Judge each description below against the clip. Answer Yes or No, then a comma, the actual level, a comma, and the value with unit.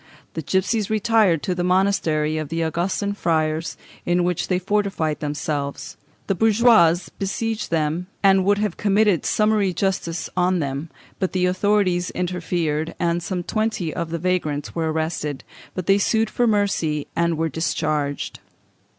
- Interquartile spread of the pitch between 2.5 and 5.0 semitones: Yes, average, 3.9 semitones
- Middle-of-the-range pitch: Yes, medium, 180 Hz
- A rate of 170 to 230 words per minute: No, average, 150 wpm